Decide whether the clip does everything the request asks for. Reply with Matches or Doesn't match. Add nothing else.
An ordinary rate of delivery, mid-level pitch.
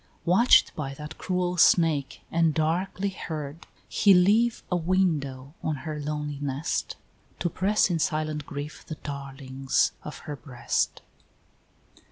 Doesn't match